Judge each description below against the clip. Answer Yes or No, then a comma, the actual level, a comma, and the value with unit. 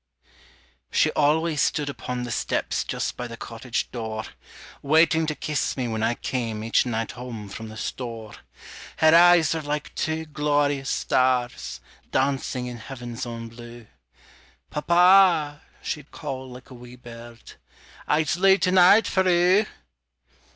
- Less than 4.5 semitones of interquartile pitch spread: No, average, 5.0 semitones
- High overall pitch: No, low, 135 Hz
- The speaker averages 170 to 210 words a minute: No, average, 140 wpm